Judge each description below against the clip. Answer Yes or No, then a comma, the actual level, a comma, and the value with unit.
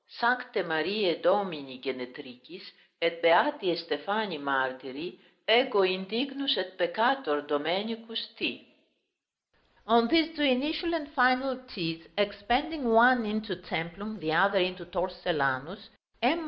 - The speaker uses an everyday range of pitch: No, wide, 6.5 semitones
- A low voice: No, high, 195 Hz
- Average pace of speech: No, slow, 110 wpm